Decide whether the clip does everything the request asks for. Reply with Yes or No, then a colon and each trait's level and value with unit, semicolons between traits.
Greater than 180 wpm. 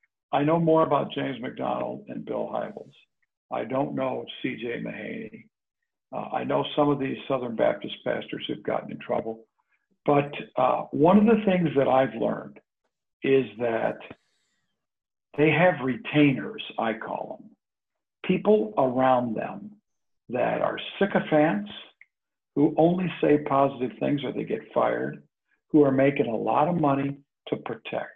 No: average, 145 wpm